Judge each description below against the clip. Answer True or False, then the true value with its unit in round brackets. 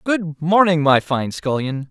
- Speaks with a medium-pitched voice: True (155 Hz)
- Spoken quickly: False (160 wpm)